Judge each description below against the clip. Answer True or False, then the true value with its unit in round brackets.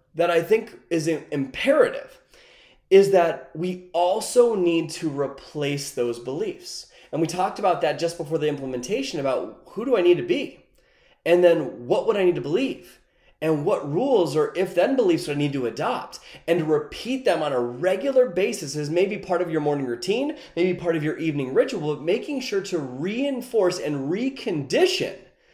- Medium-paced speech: True (185 wpm)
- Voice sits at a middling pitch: True (175 Hz)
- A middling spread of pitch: False (6.5 semitones)